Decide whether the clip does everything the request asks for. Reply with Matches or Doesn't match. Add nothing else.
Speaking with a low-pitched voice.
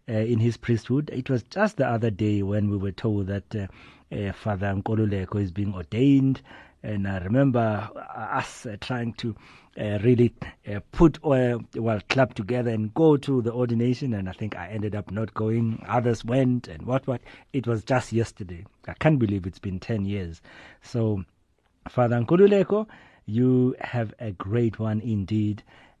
Matches